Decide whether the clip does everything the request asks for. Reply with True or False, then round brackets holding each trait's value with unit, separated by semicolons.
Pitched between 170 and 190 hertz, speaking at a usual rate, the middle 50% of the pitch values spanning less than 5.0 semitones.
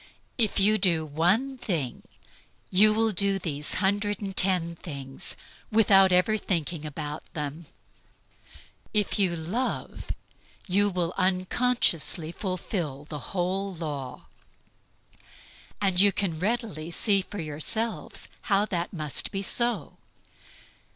False (185 Hz; 110 wpm; 4.2 semitones)